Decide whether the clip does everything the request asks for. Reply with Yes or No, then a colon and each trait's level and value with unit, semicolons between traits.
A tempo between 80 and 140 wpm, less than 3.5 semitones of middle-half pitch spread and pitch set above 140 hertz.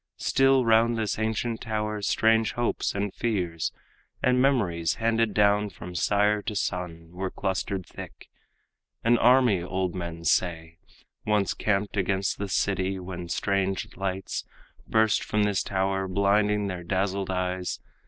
No: slow, 135 wpm; average, 2.7 semitones; low, 100 Hz